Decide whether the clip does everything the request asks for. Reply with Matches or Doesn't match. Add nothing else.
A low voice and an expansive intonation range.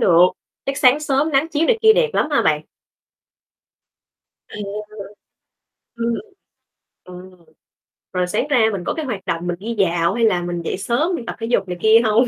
Doesn't match